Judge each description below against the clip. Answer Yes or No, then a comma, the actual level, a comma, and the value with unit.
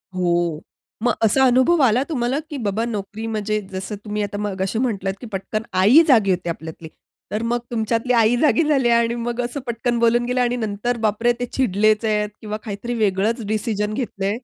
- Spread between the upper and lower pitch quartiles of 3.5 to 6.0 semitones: No, average, 2.9 semitones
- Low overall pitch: No, high, 220 Hz